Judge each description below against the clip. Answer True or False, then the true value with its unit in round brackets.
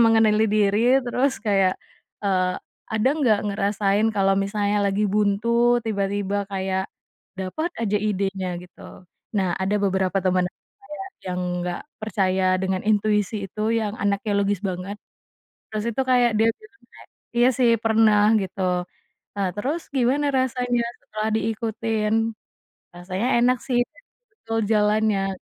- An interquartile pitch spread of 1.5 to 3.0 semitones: True (2.6 semitones)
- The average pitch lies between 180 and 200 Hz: False (210 Hz)